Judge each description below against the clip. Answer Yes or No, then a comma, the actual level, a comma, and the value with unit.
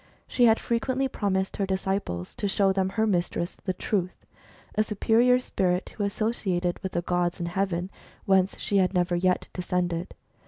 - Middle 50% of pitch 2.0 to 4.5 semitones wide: Yes, average, 2.7 semitones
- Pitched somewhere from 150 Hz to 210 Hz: Yes, high, 190 Hz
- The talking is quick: No, average, 170 wpm